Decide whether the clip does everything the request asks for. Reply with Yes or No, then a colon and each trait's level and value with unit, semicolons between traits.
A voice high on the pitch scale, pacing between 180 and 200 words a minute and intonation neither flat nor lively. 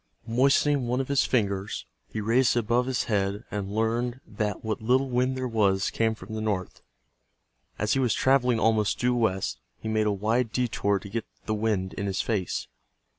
No: low, 110 Hz; average, 190 wpm; average, 3.1 semitones